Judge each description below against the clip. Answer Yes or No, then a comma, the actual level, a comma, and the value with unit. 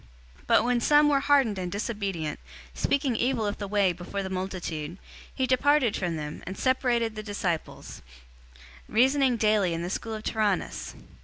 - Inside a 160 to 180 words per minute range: Yes, average, 165 wpm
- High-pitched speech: Yes, high, 215 Hz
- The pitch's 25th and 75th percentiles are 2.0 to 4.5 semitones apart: No, average, 5.2 semitones